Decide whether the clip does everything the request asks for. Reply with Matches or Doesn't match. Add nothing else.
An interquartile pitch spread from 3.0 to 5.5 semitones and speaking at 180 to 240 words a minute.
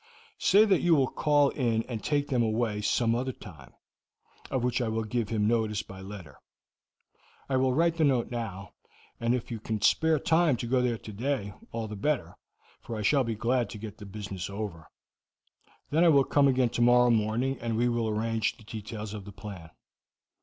Matches